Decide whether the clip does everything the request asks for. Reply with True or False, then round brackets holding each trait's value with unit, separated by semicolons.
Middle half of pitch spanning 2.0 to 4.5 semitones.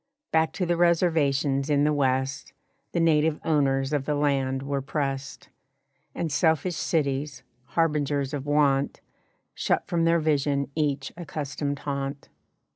True (2.4 semitones)